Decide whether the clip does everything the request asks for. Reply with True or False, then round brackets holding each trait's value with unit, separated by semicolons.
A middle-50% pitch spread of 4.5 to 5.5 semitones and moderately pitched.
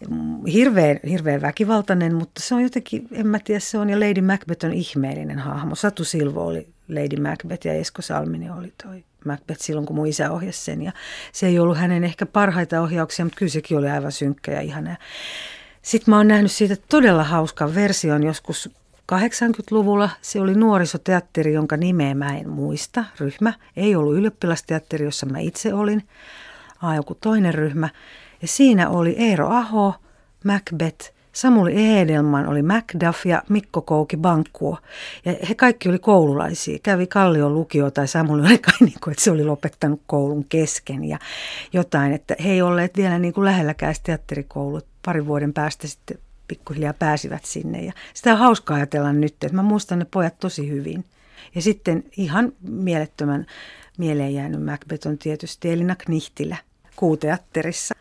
True (5.0 semitones; 170 Hz)